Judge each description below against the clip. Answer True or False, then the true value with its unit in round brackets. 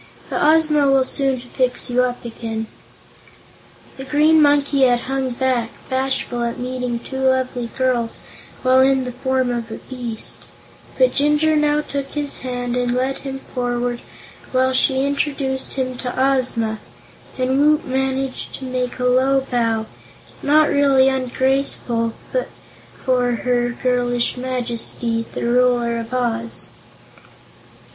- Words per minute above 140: False (135 wpm)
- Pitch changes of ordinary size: False (1.8 semitones)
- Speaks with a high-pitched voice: True (255 Hz)